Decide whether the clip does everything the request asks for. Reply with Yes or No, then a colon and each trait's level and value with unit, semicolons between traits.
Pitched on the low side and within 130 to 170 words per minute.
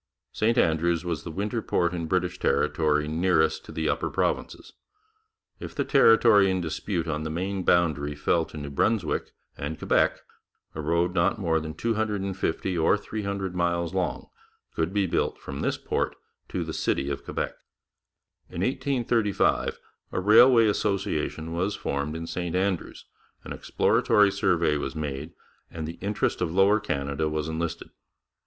Yes: very low, 85 Hz; average, 155 wpm